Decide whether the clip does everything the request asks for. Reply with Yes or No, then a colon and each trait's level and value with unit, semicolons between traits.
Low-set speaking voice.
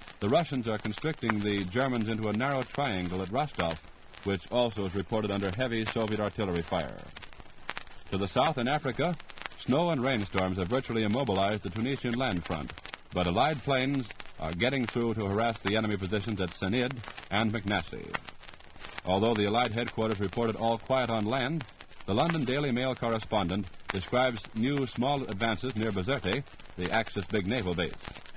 Yes: low, 110 Hz